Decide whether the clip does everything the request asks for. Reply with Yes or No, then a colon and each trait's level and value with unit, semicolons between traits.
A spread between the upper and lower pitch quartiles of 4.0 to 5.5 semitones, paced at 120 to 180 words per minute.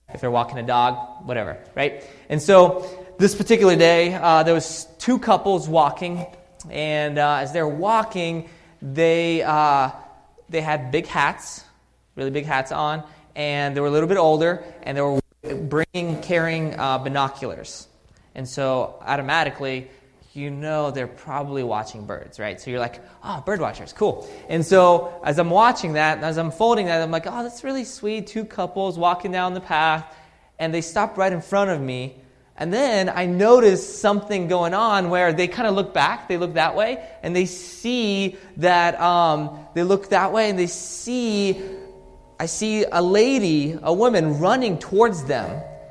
Yes: average, 4.5 semitones; average, 175 wpm